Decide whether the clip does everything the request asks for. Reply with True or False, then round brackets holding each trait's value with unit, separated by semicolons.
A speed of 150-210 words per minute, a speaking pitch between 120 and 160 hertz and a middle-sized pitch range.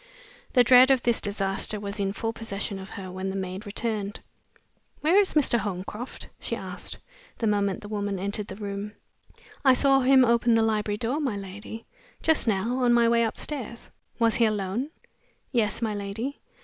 False (175 wpm; 220 Hz; 3.2 semitones)